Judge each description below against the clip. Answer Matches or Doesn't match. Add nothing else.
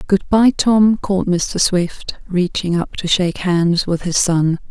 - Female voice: Matches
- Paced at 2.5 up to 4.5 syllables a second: Matches